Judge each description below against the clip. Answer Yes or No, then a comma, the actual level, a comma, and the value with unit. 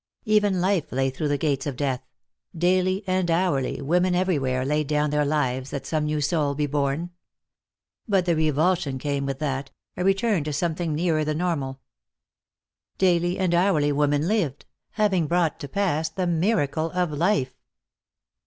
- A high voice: No, medium, 155 Hz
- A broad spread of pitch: No, average, 4.0 semitones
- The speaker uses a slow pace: No, average, 160 wpm